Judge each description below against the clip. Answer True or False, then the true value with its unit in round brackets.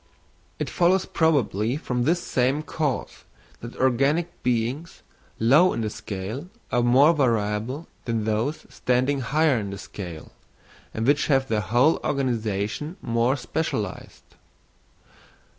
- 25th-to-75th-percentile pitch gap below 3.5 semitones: False (4.9 semitones)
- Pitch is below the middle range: True (125 Hz)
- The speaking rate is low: True (125 wpm)